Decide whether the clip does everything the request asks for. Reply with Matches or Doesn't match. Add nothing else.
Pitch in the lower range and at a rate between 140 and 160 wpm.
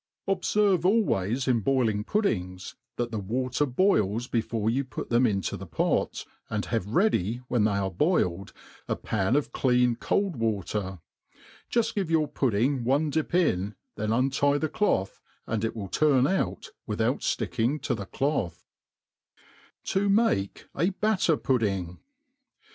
Matches